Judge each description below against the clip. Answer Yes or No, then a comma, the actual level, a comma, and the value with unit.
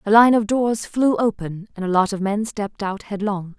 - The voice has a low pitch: No, high, 210 Hz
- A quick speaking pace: Yes, fast, 235 wpm